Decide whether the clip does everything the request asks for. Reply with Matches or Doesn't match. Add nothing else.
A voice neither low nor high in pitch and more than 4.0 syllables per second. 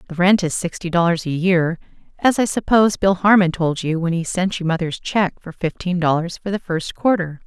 Matches